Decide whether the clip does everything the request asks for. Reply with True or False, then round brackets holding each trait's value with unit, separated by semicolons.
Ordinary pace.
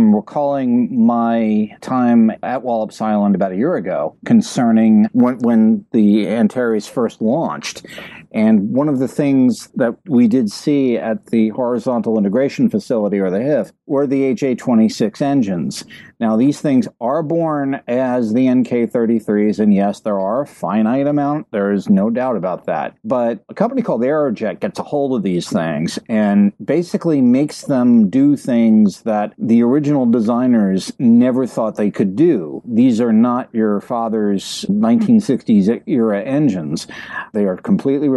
True (150 wpm)